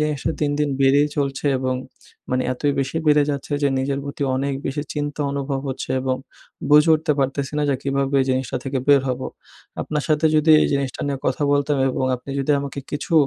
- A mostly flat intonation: Yes, narrow, 1.6 semitones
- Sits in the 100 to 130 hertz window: No, medium, 140 Hz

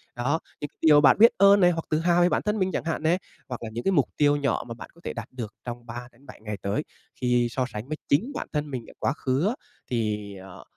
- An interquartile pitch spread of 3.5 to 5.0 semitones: No, wide, 5.5 semitones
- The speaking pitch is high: No, medium, 140 Hz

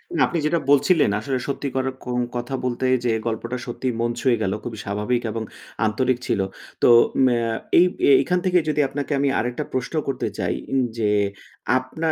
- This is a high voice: No, low, 125 Hz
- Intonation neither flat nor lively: Yes, average, 3.1 semitones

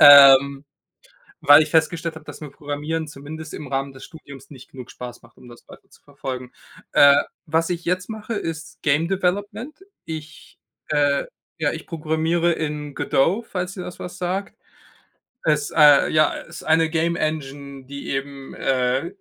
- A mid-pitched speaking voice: Yes, medium, 155 Hz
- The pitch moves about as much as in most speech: Yes, average, 3.1 semitones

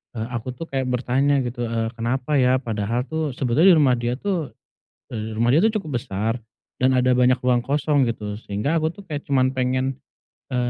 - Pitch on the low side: Yes, low, 125 Hz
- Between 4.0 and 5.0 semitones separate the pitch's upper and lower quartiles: No, average, 3.1 semitones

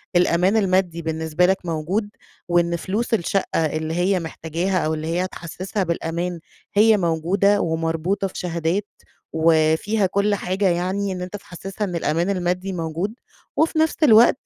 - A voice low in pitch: No, medium, 180 Hz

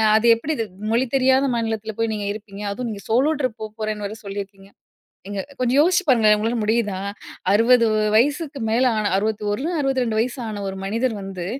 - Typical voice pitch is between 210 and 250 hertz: Yes, high, 220 Hz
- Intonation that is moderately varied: Yes, average, 3.5 semitones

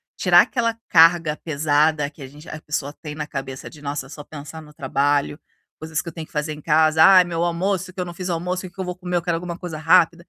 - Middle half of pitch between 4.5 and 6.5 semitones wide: No, average, 2.8 semitones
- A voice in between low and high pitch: Yes, medium, 160 Hz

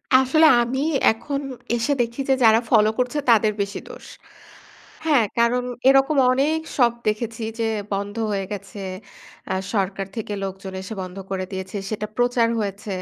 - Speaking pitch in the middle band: No, high, 225 Hz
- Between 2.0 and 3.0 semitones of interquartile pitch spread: No, average, 3.8 semitones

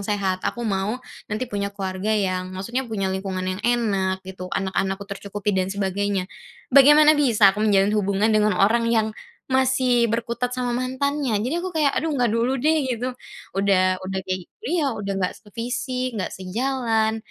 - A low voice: No, high, 215 Hz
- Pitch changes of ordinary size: Yes, average, 4.6 semitones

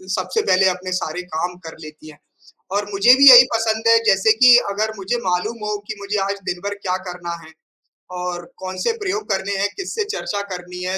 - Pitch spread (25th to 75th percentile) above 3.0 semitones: Yes, average, 3.5 semitones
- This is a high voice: Yes, high, 195 Hz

